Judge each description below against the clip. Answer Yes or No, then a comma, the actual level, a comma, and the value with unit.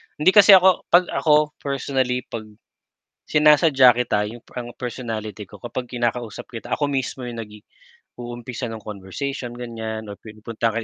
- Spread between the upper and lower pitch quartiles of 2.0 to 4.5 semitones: Yes, average, 3.6 semitones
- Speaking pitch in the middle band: No, low, 120 Hz